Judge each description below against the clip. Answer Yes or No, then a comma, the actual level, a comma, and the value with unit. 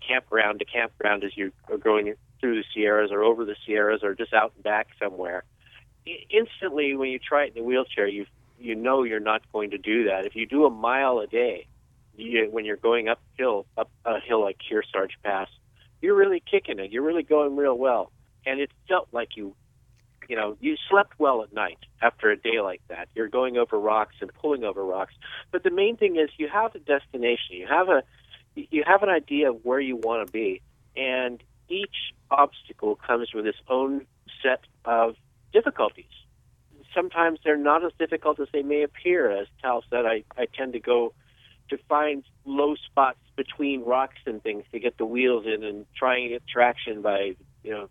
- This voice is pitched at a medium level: No, low, 125 Hz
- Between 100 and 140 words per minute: No, average, 200 wpm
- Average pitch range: Yes, average, 4.6 semitones